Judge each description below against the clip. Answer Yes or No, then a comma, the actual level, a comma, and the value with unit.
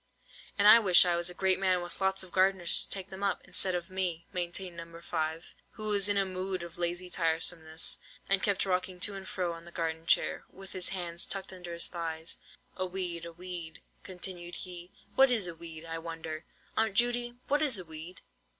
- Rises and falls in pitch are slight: Yes, narrow, 2.2 semitones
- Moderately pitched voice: Yes, medium, 180 Hz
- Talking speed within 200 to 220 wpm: Yes, fast, 205 wpm